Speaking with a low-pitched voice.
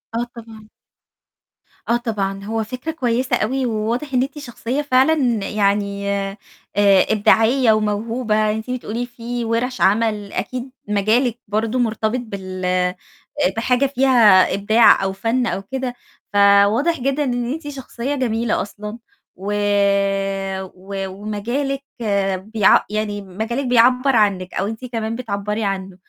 No: high, 225 Hz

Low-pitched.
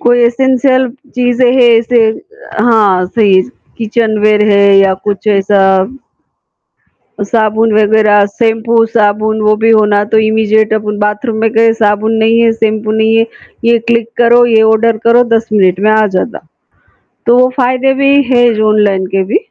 No: high, 220 Hz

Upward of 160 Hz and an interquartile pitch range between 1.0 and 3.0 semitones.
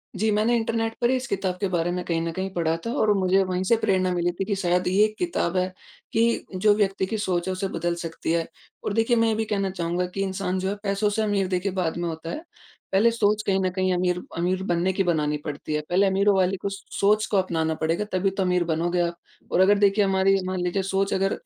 Yes: high, 190 Hz; narrow, 2.4 semitones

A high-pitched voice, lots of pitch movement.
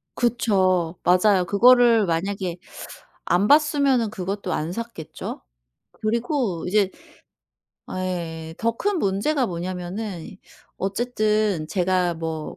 No: high, 195 Hz; average, 4.6 semitones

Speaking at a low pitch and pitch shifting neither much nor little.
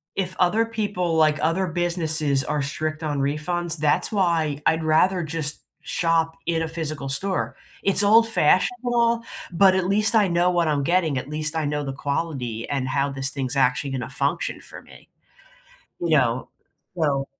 No: medium, 160 Hz; average, 3.9 semitones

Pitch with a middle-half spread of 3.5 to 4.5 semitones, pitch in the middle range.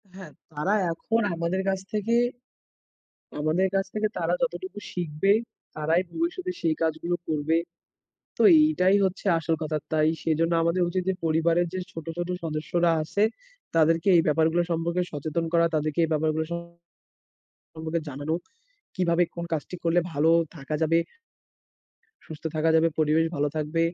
No: narrow, 2.4 semitones; medium, 165 Hz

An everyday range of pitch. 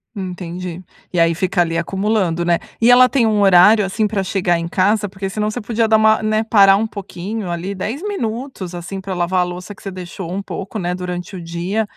Yes: average, 3.3 semitones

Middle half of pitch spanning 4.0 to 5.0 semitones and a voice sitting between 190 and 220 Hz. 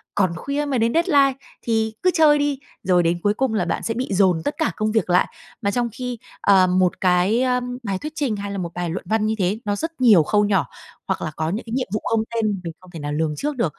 No: wide, 5.5 semitones; high, 210 Hz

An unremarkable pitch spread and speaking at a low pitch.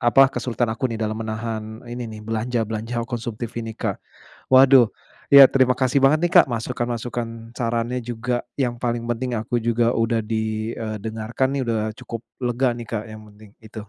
No: narrow, 1.7 semitones; low, 115 Hz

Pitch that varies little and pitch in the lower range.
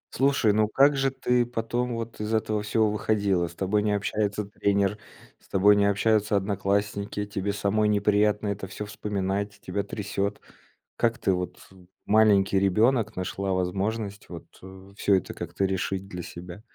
Yes: narrow, 1.7 semitones; low, 100 Hz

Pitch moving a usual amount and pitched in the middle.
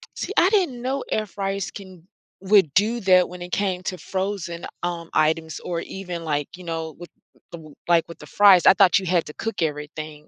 Yes: average, 3.2 semitones; medium, 180 Hz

